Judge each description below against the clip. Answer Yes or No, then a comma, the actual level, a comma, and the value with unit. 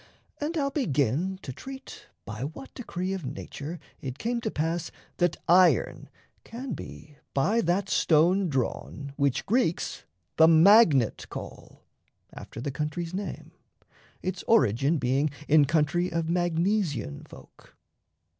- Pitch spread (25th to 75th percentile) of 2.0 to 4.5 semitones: No, average, 5.2 semitones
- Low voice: No, medium, 165 Hz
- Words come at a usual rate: No, slow, 125 wpm